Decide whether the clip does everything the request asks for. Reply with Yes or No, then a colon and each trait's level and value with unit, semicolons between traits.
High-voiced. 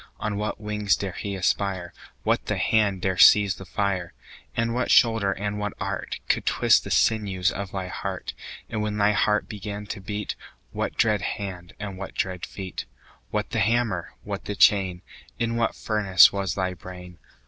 No: low, 100 Hz